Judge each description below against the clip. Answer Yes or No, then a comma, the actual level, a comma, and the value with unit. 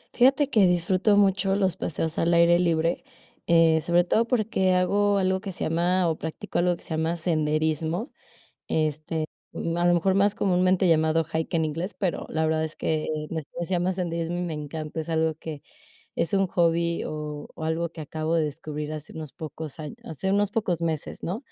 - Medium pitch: Yes, medium, 170 Hz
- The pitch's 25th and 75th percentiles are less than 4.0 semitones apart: Yes, average, 2.7 semitones